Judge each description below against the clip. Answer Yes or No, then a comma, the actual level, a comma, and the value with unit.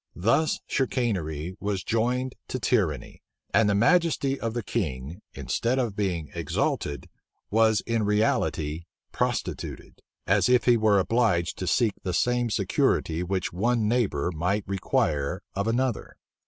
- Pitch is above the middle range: No, low, 105 Hz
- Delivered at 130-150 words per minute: Yes, slow, 135 wpm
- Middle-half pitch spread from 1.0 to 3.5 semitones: No, average, 5.1 semitones